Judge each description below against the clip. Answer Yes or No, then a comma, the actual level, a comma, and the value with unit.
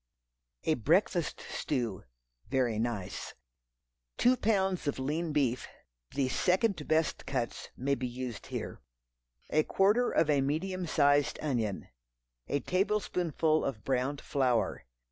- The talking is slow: Yes, slow, 120 wpm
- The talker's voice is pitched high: No, medium, 145 Hz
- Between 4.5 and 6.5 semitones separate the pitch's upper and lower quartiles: Yes, wide, 5.5 semitones